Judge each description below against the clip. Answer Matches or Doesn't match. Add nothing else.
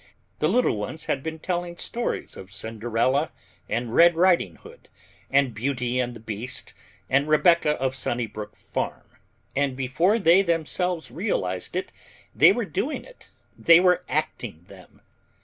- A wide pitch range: Matches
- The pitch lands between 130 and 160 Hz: Matches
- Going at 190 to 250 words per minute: Doesn't match